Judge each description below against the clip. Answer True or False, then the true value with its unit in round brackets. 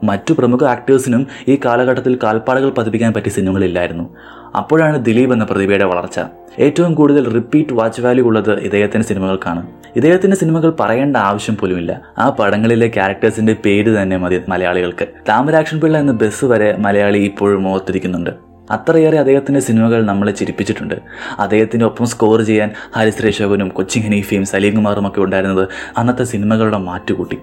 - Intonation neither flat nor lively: True (4.1 semitones)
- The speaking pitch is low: True (110 Hz)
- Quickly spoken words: True (130 wpm)